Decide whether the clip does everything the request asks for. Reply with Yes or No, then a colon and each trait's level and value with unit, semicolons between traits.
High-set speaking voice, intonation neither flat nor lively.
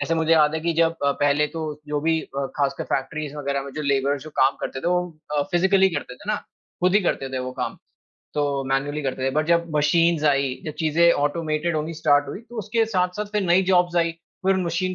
No: medium, 155 Hz; average, 3.2 semitones